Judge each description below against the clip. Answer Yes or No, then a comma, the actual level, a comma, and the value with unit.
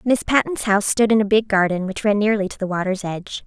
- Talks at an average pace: No, fast, 260 wpm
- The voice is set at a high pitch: Yes, high, 205 Hz